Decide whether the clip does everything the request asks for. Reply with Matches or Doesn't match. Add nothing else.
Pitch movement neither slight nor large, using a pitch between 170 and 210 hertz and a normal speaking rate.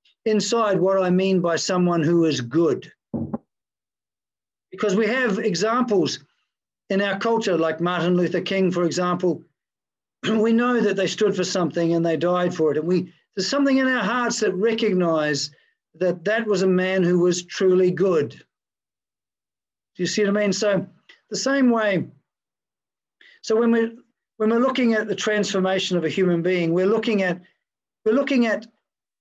Matches